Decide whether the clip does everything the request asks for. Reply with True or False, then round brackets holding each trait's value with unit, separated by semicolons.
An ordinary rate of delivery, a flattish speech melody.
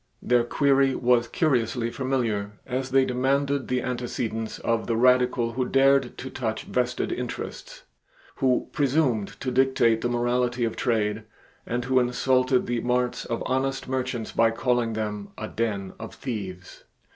True (145 wpm; 2.3 semitones)